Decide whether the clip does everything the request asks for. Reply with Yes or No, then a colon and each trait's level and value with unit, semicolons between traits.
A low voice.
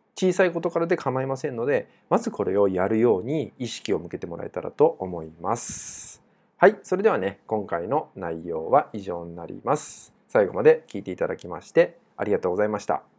Yes: low, 120 Hz